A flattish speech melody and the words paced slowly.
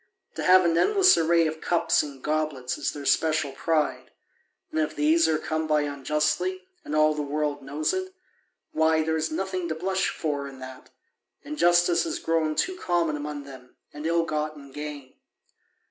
No: narrow, 2.3 semitones; average, 175 wpm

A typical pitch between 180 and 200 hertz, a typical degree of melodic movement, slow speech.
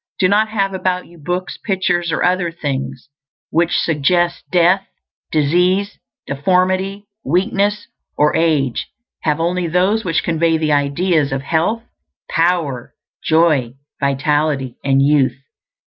No: medium, 170 Hz; average, 3.9 semitones; slow, 120 wpm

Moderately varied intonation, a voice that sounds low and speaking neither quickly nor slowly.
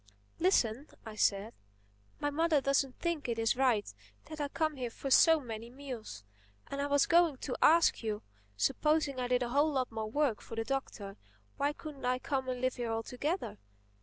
No: average, 4.4 semitones; very high, 260 Hz; average, 185 wpm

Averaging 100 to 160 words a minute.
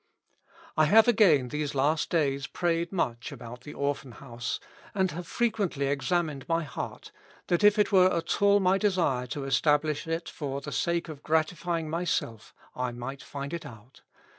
No: average, 170 wpm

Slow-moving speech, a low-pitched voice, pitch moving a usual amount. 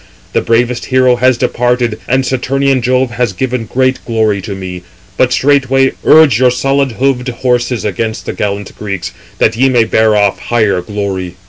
No: average, 165 wpm; low, 120 Hz; average, 3.3 semitones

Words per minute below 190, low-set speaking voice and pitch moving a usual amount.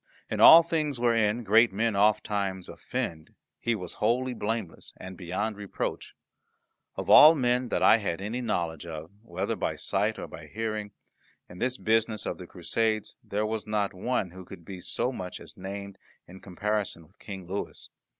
Yes: average, 170 wpm; low, 105 Hz; average, 3.4 semitones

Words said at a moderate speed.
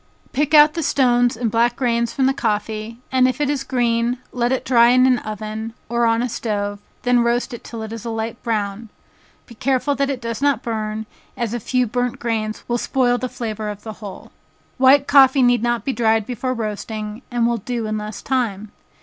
No: fast, 210 wpm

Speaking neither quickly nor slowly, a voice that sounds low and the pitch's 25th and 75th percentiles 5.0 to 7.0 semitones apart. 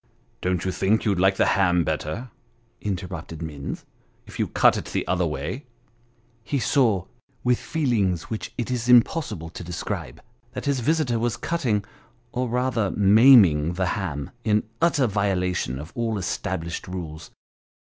Yes: average, 155 wpm; low, 100 Hz; wide, 5.5 semitones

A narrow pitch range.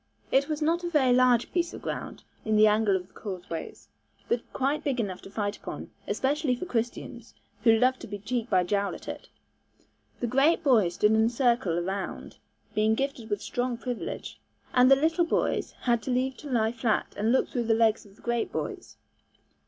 No: average, 3.7 semitones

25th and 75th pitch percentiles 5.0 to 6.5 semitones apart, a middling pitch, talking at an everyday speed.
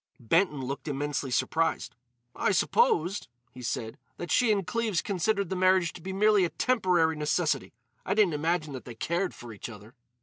Yes: wide, 5.5 semitones; medium, 170 Hz; average, 175 wpm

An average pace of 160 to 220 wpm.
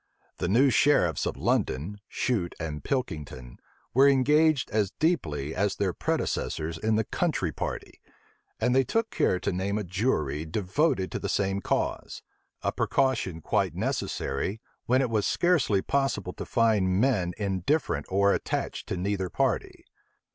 No: average, 145 wpm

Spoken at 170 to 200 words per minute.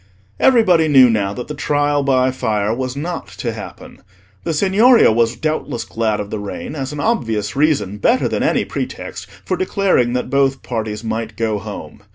Yes: average, 180 wpm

